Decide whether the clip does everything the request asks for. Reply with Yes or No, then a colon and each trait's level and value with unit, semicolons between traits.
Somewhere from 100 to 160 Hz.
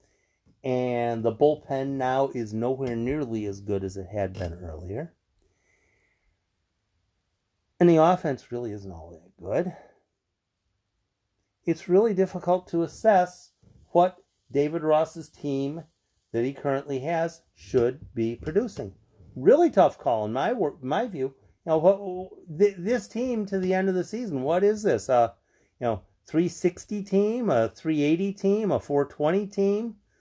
Yes: medium, 140 Hz